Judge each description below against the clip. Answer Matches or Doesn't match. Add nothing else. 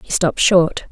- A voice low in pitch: Doesn't match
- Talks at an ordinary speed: Matches